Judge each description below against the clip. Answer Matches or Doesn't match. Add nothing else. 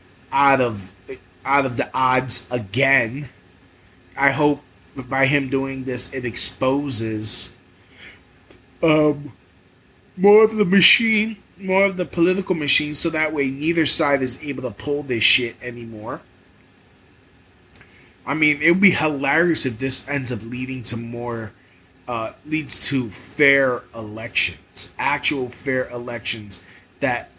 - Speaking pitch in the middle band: Doesn't match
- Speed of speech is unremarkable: Doesn't match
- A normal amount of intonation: Matches